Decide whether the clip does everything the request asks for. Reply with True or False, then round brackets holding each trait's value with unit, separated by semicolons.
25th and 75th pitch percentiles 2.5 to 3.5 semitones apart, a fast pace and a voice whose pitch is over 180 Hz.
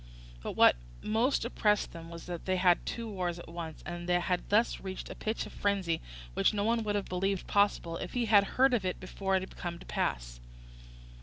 True (3.2 semitones; 215 wpm; 190 Hz)